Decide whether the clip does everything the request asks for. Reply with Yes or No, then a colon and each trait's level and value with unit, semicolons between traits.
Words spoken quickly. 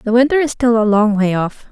Yes: fast, 280 wpm